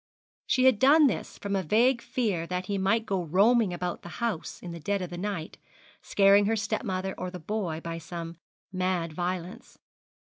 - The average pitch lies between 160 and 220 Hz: Yes, high, 190 Hz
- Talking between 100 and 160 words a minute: No, average, 185 wpm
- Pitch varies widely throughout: No, average, 3.9 semitones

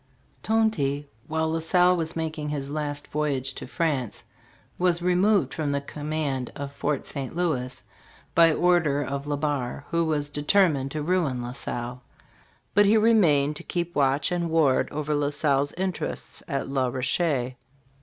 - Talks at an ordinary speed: Yes, average, 160 wpm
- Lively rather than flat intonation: No, average, 3.2 semitones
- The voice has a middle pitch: Yes, medium, 150 Hz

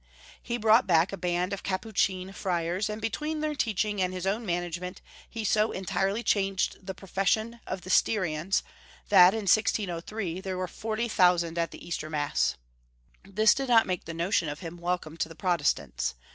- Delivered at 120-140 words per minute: No, average, 175 wpm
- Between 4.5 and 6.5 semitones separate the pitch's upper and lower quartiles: No, average, 3.7 semitones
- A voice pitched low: No, high, 190 Hz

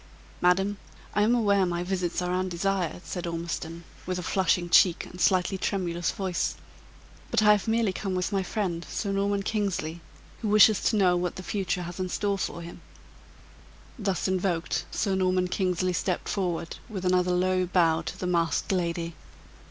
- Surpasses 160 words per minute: Yes, average, 170 wpm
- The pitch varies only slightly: Yes, narrow, 2.0 semitones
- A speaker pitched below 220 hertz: Yes, medium, 185 Hz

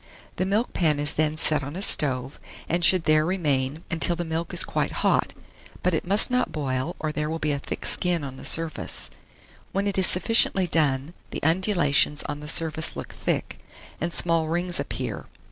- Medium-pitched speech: Yes, medium, 160 Hz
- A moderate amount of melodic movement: Yes, average, 3.0 semitones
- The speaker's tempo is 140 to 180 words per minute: No, average, 190 wpm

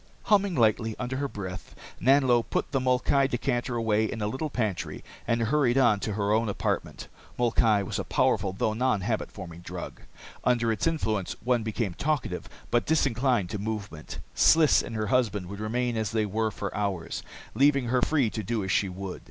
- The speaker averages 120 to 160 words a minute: No, average, 185 wpm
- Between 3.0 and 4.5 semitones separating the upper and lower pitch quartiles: Yes, average, 3.6 semitones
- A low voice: Yes, low, 115 Hz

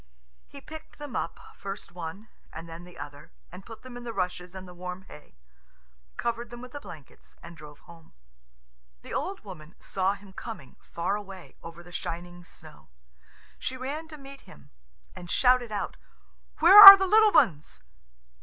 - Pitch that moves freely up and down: Yes, wide, 6.7 semitones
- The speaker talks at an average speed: Yes, average, 175 wpm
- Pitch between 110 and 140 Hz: No, high, 190 Hz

